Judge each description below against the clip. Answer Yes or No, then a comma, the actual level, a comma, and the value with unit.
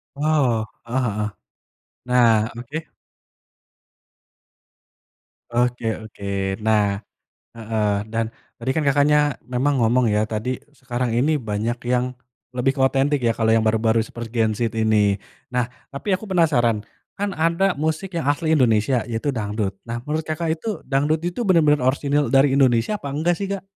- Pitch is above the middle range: No, low, 125 Hz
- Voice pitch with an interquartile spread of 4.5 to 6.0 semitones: Yes, average, 4.9 semitones